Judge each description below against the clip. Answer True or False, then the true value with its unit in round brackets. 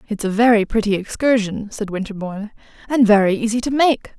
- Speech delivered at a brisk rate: False (170 wpm)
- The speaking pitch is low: False (215 Hz)